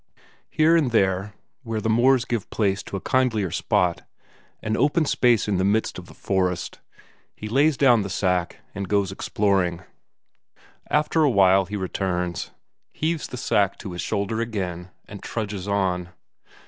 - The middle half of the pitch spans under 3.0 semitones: No, average, 3.9 semitones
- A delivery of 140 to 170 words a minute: Yes, average, 160 wpm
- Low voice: Yes, low, 100 Hz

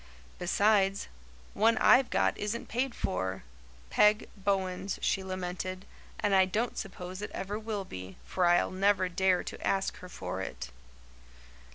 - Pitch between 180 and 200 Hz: Yes, high, 190 Hz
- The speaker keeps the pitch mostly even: Yes, narrow, 2.3 semitones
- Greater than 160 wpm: No, average, 145 wpm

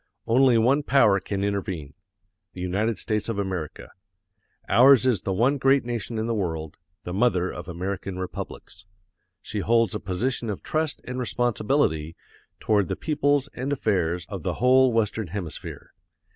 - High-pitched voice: No, low, 110 Hz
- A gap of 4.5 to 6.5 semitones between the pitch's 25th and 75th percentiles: Yes, average, 5.2 semitones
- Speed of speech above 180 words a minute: No, average, 155 wpm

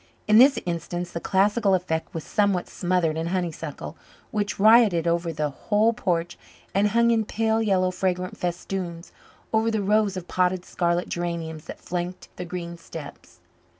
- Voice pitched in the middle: Yes, medium, 180 Hz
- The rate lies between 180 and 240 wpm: No, average, 155 wpm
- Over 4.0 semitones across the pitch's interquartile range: No, average, 3.3 semitones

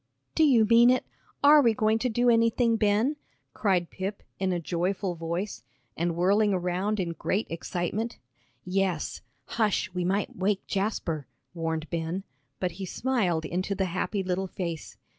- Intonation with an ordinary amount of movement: Yes, average, 3.8 semitones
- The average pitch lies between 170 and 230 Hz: Yes, high, 190 Hz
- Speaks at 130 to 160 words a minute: Yes, average, 155 wpm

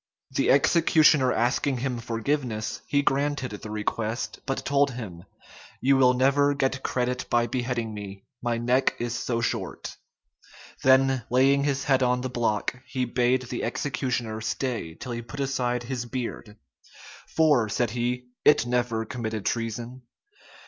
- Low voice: Yes, low, 125 Hz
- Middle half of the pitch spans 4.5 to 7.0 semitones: No, narrow, 2.4 semitones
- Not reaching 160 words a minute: Yes, average, 145 wpm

